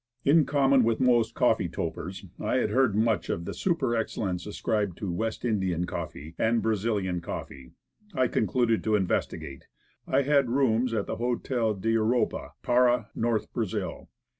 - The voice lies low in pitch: Yes, low, 115 Hz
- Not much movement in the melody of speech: No, average, 3.5 semitones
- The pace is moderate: Yes, average, 155 wpm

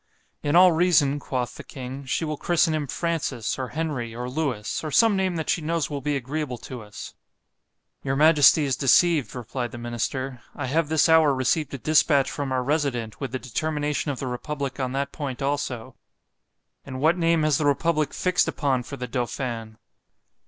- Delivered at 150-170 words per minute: No, average, 180 wpm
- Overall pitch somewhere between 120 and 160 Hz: Yes, medium, 140 Hz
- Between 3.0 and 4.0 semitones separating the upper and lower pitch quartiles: Yes, average, 3.5 semitones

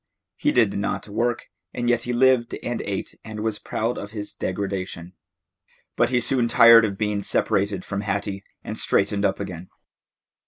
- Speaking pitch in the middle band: No, low, 105 Hz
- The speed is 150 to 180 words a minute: Yes, average, 165 wpm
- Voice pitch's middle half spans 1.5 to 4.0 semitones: Yes, average, 3.0 semitones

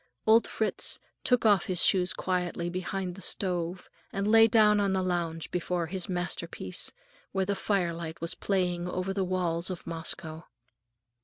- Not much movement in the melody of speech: Yes, narrow, 2.1 semitones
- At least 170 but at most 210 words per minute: No, average, 155 wpm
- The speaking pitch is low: No, medium, 185 Hz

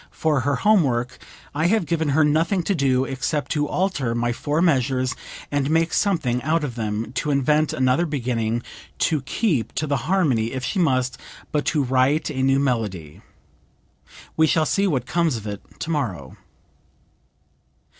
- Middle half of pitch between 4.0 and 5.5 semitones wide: Yes, average, 4.3 semitones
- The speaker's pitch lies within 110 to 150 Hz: Yes, medium, 140 Hz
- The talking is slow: No, average, 165 wpm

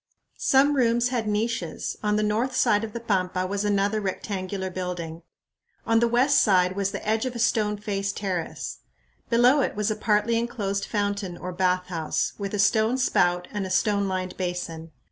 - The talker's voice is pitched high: Yes, high, 205 Hz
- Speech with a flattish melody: No, average, 3.5 semitones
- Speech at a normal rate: Yes, average, 180 wpm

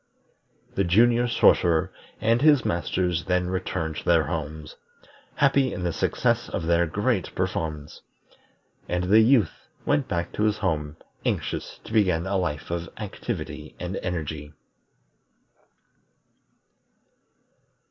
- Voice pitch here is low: Yes, very low, 90 Hz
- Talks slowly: Yes, slow, 120 wpm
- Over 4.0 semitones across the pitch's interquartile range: Yes, average, 5.0 semitones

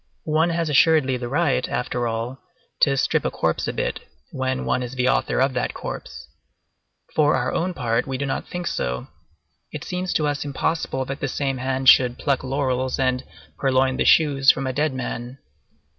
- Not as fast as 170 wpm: No, average, 190 wpm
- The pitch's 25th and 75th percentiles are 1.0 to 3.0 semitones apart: Yes, narrow, 2.5 semitones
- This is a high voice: No, low, 135 Hz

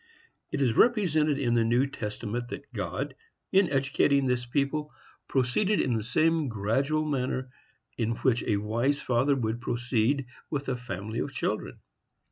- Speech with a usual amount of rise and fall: Yes, average, 3.4 semitones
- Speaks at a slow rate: No, average, 150 wpm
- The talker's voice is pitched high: No, low, 130 Hz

